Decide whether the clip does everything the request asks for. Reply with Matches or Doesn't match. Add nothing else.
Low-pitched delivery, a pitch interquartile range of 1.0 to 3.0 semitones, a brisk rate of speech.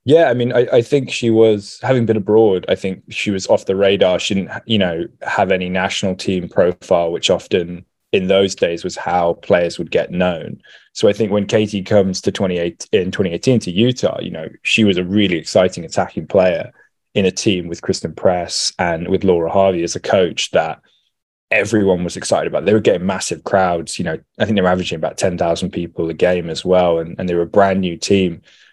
Matches